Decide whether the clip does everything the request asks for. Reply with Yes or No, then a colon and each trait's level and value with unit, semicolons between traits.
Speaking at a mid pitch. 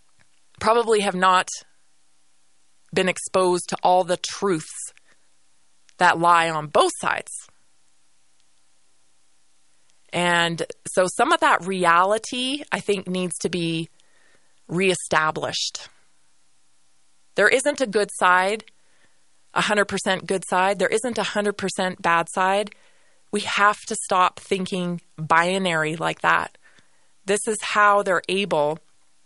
Yes: medium, 175 Hz